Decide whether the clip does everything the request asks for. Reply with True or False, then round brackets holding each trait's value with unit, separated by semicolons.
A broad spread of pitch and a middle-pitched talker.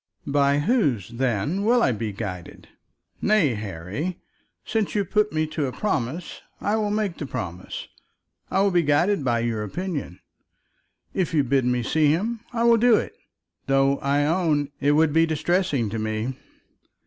True (7.5 semitones; 145 Hz)